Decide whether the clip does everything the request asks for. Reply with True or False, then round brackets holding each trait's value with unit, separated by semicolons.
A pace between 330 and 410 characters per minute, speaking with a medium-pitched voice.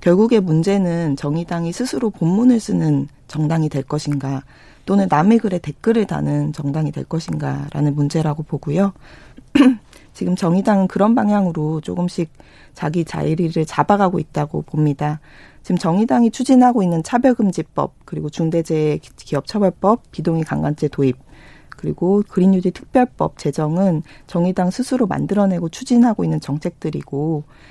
True (335 characters per minute; 170 Hz)